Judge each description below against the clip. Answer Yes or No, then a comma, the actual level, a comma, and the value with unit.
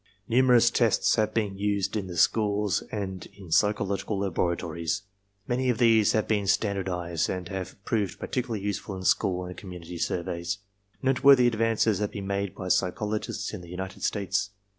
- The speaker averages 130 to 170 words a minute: Yes, average, 160 wpm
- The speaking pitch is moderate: No, low, 100 Hz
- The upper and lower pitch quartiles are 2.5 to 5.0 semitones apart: Yes, average, 2.9 semitones